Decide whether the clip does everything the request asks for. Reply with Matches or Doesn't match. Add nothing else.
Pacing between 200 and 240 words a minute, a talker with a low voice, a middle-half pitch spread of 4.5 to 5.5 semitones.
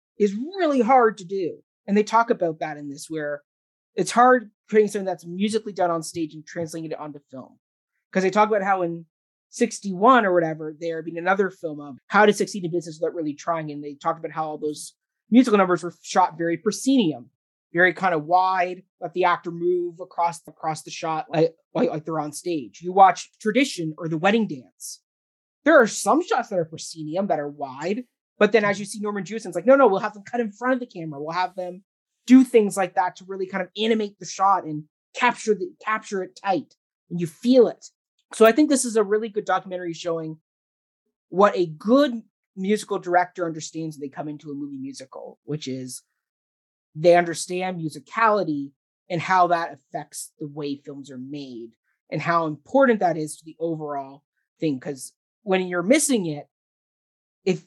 Doesn't match